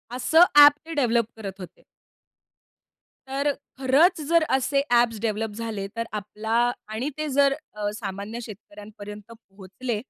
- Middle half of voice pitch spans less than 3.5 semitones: No, average, 4.2 semitones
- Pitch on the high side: Yes, high, 230 Hz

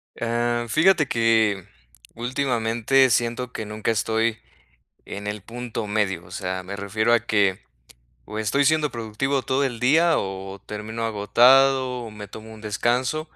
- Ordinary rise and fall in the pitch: Yes, average, 3.1 semitones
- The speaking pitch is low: Yes, low, 115 Hz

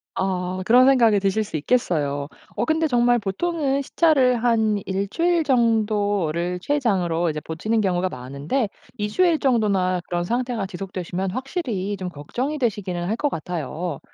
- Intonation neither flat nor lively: No, wide, 5.8 semitones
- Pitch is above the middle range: Yes, high, 205 Hz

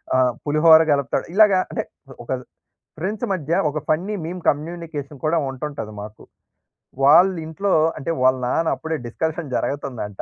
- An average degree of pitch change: Yes, average, 3.6 semitones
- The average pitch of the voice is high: No, medium, 155 Hz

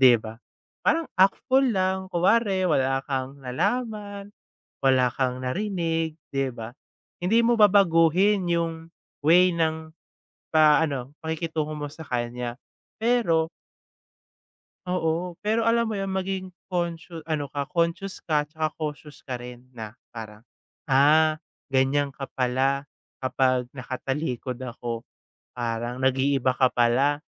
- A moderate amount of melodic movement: No, wide, 5.8 semitones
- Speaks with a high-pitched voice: No, medium, 155 Hz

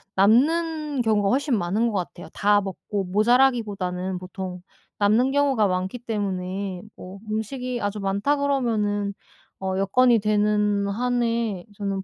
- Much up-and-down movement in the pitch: No, average, 3.9 semitones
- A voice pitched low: No, high, 210 Hz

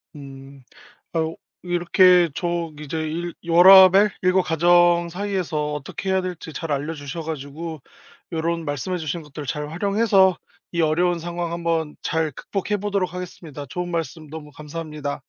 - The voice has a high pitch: No, medium, 165 Hz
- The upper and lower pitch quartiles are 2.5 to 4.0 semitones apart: Yes, average, 2.8 semitones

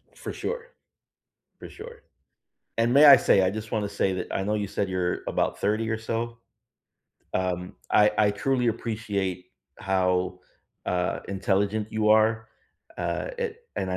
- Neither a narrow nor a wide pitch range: Yes, average, 3.1 semitones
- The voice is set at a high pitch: No, low, 105 Hz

